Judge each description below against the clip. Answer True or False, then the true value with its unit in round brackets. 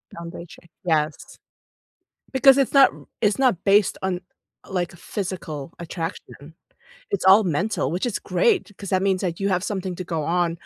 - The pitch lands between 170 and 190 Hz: True (185 Hz)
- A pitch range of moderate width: True (3.2 semitones)